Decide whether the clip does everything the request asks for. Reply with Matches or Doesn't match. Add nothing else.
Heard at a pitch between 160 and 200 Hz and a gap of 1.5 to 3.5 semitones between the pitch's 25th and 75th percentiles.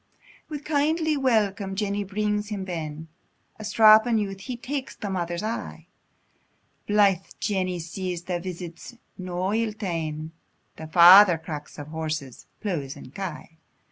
Doesn't match